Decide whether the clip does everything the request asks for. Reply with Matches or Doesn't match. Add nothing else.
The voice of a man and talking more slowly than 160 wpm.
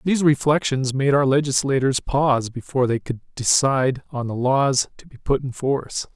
Doesn't match